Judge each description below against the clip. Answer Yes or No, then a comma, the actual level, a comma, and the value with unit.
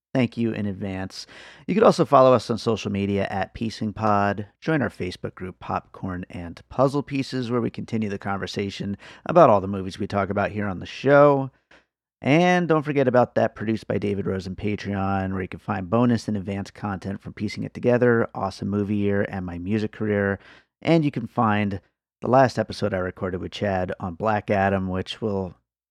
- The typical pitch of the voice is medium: No, low, 105 Hz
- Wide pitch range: No, average, 3.3 semitones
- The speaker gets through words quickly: No, average, 190 wpm